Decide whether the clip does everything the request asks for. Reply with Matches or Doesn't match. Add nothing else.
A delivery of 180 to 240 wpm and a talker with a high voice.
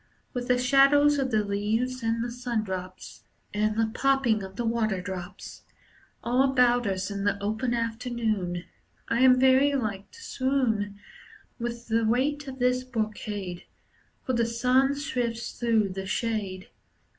Doesn't match